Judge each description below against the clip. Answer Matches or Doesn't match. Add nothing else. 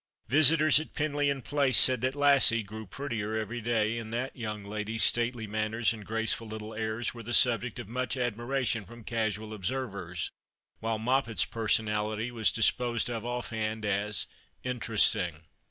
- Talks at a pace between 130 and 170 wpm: Matches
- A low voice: Matches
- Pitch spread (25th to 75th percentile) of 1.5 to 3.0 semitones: Matches